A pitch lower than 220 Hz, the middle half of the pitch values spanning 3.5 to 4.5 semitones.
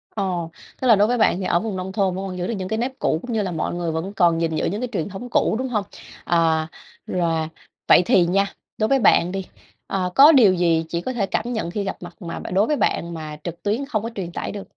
Yes: high, 190 Hz; average, 4.2 semitones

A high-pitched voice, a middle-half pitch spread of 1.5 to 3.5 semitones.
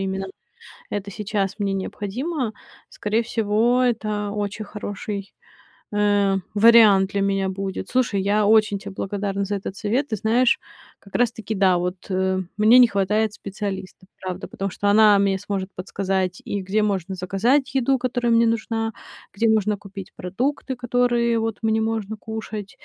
Yes: high, 205 Hz; narrow, 2.5 semitones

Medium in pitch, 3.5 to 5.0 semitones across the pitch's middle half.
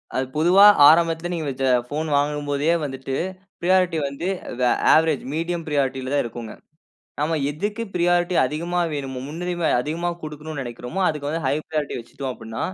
Yes: medium, 150 Hz; average, 3.9 semitones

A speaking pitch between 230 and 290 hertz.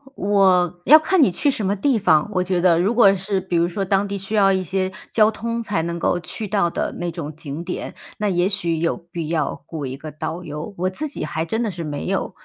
No: medium, 185 Hz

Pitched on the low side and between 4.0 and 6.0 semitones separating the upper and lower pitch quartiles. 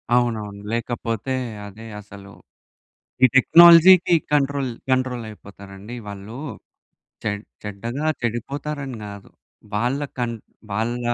Yes: low, 120 Hz; average, 4.4 semitones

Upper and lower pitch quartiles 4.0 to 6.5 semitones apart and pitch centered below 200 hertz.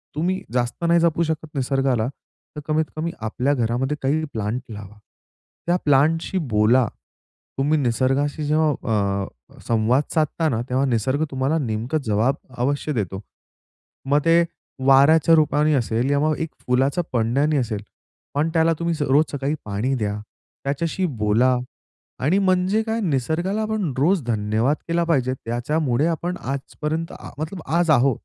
Yes: average, 4.6 semitones; medium, 140 Hz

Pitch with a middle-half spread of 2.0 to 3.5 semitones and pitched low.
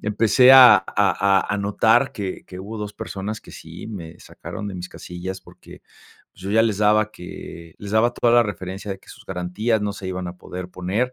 Yes: average, 2.8 semitones; low, 100 Hz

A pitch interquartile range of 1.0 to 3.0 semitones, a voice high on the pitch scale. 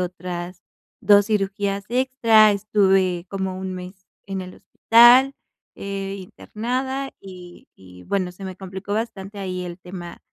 Yes: narrow, 2.5 semitones; high, 195 Hz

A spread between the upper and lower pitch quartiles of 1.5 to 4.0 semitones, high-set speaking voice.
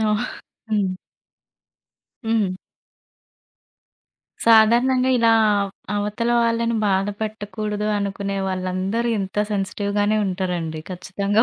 Yes: average, 2.7 semitones; high, 205 Hz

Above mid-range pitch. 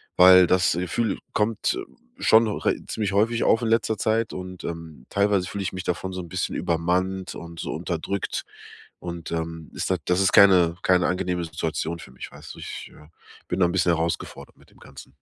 No: very low, 90 Hz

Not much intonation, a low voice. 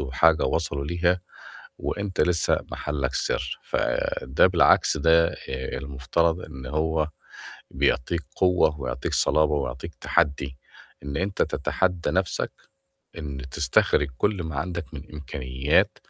No: average, 3.8 semitones; very low, 75 Hz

